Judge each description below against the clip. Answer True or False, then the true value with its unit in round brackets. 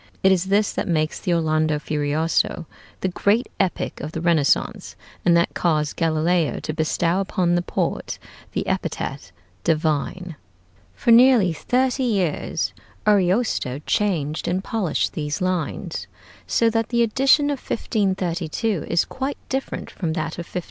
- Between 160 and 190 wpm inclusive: False (140 wpm)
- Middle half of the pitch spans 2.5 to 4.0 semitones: False (4.9 semitones)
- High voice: False (175 Hz)